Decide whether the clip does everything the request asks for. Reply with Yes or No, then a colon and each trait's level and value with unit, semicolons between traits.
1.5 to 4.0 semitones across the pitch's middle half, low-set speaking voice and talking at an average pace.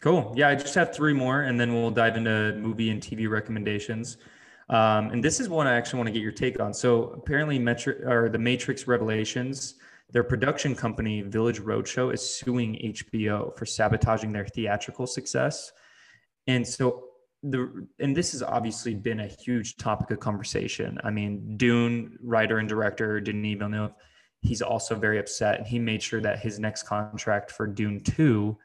Yes: average, 2.7 semitones; low, 115 Hz; average, 180 wpm